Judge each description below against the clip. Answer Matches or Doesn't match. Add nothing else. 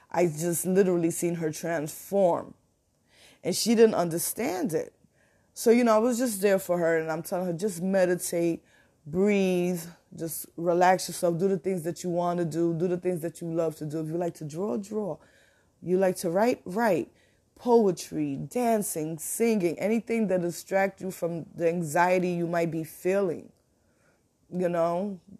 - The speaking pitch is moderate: Matches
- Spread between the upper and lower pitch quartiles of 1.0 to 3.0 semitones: Matches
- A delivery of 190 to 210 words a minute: Doesn't match